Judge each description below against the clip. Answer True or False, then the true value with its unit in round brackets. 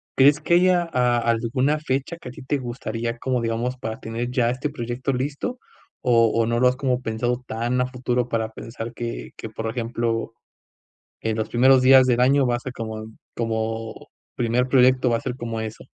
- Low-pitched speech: True (120 Hz)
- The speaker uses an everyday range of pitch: False (2.2 semitones)